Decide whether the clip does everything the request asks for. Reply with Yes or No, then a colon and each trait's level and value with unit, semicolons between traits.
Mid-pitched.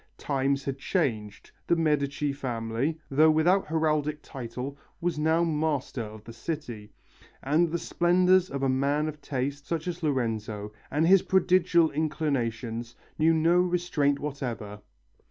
Yes: medium, 150 Hz